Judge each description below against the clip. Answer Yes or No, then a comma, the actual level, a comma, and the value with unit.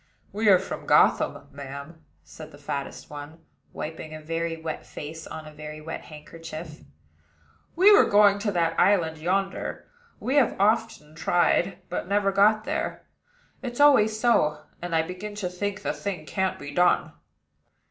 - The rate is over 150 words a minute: Yes, average, 160 wpm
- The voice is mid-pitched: Yes, medium, 175 Hz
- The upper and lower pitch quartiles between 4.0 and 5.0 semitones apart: Yes, average, 4.7 semitones